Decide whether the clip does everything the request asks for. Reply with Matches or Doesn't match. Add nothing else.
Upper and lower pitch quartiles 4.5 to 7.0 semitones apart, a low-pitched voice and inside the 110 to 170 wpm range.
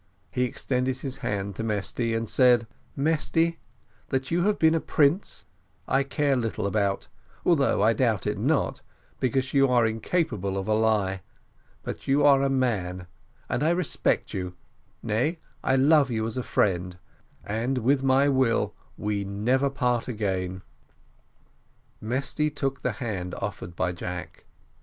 Matches